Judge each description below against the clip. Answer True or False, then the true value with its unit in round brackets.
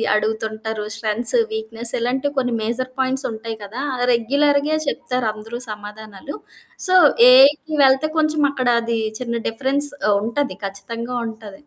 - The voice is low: False (235 Hz)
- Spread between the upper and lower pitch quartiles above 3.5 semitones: True (3.9 semitones)